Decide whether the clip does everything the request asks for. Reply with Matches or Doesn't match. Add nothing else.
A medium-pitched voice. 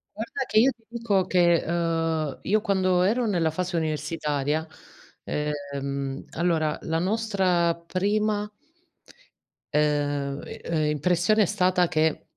Matches